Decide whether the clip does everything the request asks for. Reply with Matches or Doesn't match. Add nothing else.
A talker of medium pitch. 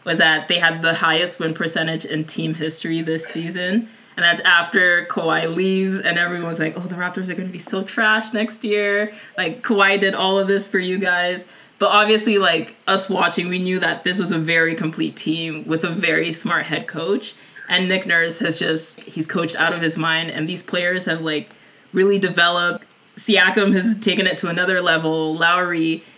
Matches